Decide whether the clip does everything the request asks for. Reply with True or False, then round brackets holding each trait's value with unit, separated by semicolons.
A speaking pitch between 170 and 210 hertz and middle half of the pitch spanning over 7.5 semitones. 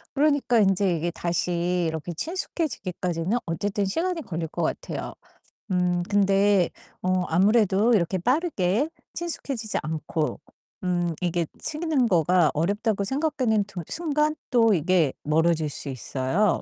False (190 Hz; 5.6 semitones)